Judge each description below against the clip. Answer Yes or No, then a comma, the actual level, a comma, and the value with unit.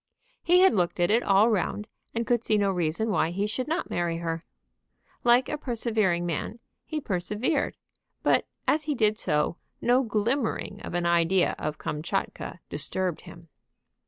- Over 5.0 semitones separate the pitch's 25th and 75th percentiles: Yes, wide, 5.5 semitones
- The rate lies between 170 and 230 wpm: No, average, 160 wpm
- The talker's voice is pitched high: Yes, high, 205 Hz